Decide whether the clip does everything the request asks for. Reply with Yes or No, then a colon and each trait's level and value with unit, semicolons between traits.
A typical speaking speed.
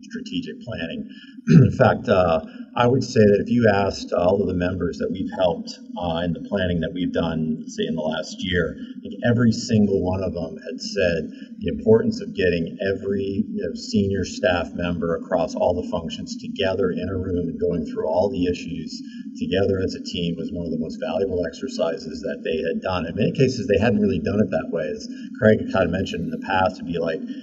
No: fast, 220 wpm